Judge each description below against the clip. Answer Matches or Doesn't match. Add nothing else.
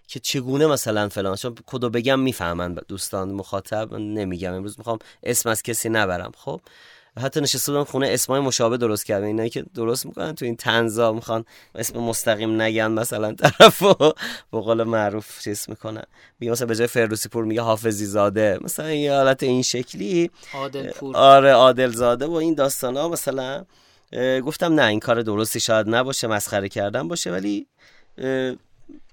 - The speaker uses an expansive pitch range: Doesn't match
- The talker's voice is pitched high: Doesn't match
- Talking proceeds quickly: Matches